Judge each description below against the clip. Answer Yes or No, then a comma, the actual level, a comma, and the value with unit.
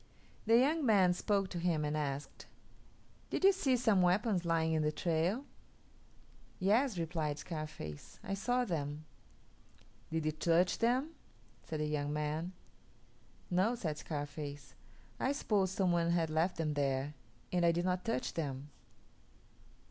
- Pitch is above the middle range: No, medium, 170 Hz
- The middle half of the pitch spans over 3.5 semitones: Yes, average, 4.6 semitones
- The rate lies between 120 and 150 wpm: Yes, average, 145 wpm